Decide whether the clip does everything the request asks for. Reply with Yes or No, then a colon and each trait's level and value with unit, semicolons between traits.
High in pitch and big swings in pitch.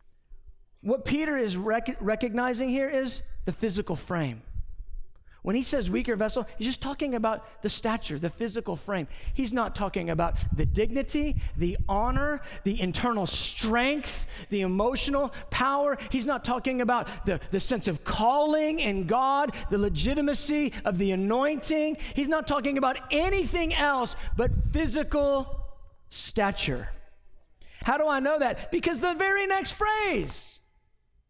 Yes: high, 240 Hz; wide, 6.4 semitones